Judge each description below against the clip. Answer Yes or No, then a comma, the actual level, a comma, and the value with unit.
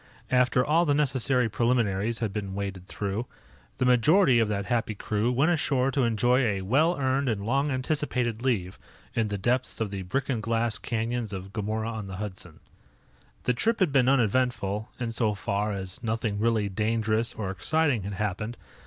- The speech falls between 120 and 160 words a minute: No, average, 180 wpm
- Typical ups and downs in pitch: Yes, average, 3.8 semitones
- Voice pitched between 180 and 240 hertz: No, low, 115 Hz